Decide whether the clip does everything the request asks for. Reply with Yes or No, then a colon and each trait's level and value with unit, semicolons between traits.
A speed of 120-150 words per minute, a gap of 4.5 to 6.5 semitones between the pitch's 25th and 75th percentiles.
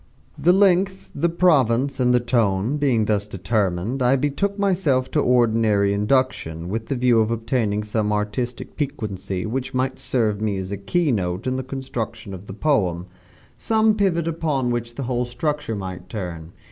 No: average, 170 wpm; average, 5.0 semitones